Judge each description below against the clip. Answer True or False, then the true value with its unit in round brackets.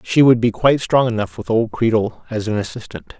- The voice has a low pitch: True (115 Hz)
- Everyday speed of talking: False (225 wpm)